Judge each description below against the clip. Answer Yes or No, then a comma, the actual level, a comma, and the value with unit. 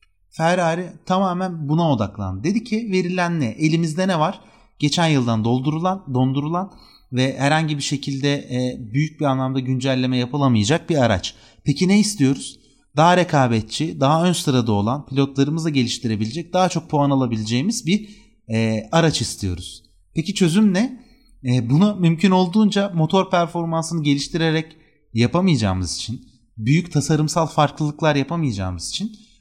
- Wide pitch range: Yes, wide, 5.8 semitones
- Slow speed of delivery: No, average, 130 wpm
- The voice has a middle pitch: Yes, medium, 150 Hz